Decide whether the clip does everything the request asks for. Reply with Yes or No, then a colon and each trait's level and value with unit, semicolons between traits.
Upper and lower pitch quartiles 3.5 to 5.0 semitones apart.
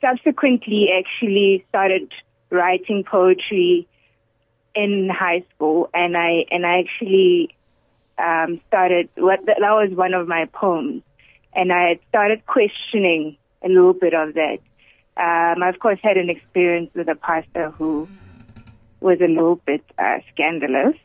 No: average, 3.1 semitones